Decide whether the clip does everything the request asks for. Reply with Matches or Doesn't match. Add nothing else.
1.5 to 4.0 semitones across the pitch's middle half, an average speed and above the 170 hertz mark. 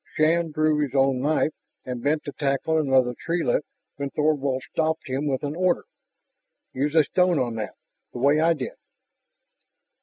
Doesn't match